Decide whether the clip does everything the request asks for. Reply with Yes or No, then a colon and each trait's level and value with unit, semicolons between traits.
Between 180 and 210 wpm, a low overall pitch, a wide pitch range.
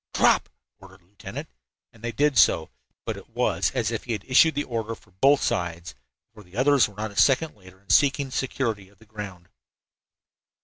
Yes: fast, 205 wpm; low, 110 Hz; wide, 5.7 semitones